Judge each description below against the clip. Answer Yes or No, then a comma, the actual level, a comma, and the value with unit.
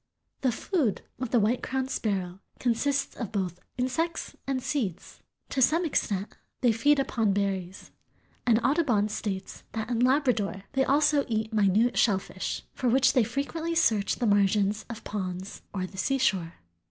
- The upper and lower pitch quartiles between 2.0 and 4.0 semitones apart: No, average, 5.1 semitones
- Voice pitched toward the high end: Yes, high, 225 Hz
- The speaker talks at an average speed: Yes, average, 155 wpm